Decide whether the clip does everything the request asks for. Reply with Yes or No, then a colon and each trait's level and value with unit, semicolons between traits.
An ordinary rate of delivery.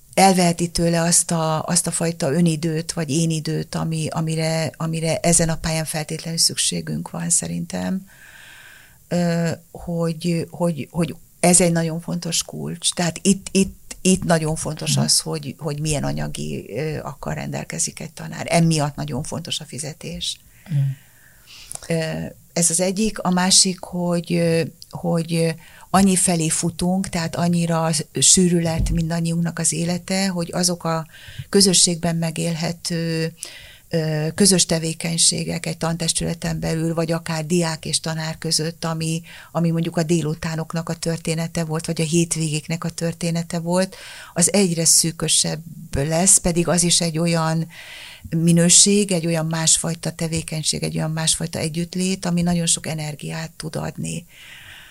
Yes: average, 130 wpm